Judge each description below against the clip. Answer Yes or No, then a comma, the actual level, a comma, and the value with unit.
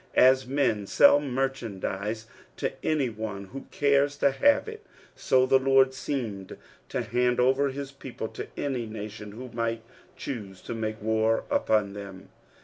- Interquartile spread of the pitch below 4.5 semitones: Yes, average, 3.8 semitones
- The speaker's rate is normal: Yes, average, 150 wpm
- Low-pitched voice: Yes, low, 125 Hz